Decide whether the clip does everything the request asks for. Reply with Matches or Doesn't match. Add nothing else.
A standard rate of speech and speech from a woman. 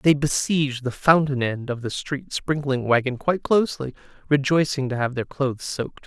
Doesn't match